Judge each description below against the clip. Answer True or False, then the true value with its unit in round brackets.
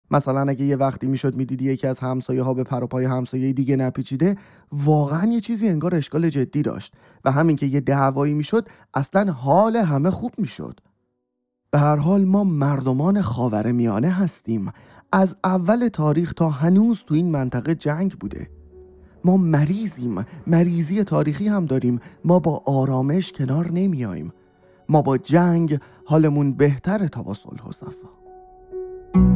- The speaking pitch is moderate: True (150 Hz)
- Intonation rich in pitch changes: True (5.8 semitones)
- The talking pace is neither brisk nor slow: True (145 wpm)